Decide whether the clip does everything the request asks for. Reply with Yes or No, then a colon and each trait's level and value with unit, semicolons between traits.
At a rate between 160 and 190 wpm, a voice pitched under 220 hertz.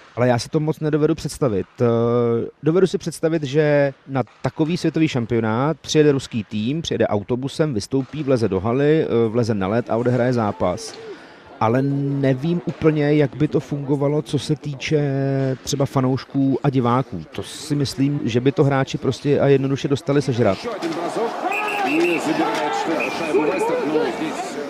No: average, 135 wpm; medium, 140 Hz